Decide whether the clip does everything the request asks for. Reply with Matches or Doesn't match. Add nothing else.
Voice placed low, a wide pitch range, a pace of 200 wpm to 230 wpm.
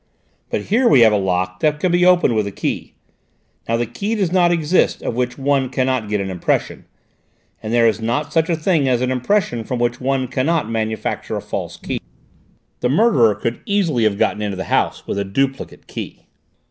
Matches